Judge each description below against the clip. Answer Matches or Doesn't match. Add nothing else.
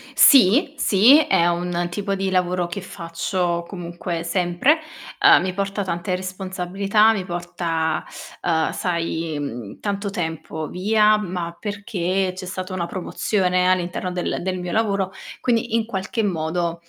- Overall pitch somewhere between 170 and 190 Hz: Matches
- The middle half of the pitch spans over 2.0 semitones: Matches